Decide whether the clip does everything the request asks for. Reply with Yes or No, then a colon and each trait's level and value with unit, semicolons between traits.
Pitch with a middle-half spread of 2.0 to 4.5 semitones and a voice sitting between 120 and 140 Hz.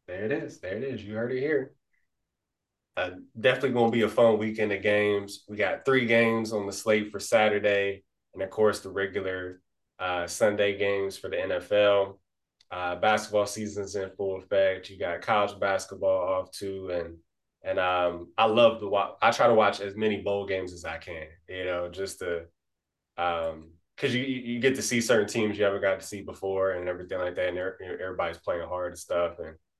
No: average, 2.8 semitones; low, 100 Hz